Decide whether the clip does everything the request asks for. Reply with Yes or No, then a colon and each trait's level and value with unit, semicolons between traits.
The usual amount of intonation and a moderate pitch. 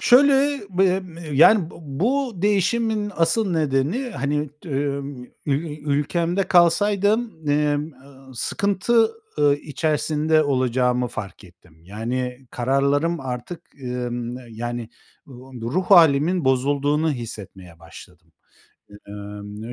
No: wide, 6.0 semitones; medium, 145 Hz